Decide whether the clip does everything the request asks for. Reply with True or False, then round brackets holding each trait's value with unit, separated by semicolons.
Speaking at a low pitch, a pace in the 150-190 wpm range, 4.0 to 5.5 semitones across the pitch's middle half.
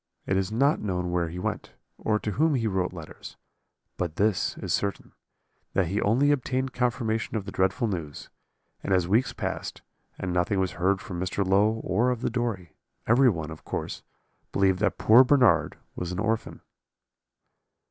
True (100 Hz; 175 wpm; 4.3 semitones)